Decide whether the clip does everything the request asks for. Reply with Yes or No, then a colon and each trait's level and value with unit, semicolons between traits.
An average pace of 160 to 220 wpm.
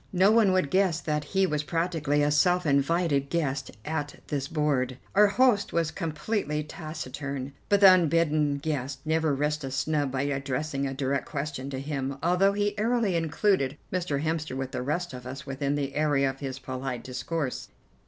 Yes: average, 175 wpm